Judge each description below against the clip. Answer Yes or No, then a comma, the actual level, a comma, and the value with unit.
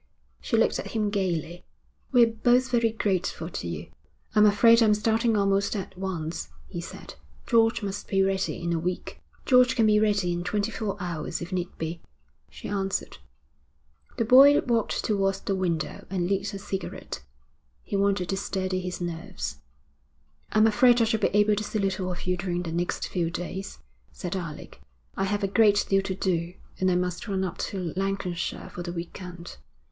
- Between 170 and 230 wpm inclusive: Yes, average, 185 wpm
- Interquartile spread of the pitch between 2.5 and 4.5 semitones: Yes, average, 3.0 semitones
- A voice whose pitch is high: Yes, high, 195 Hz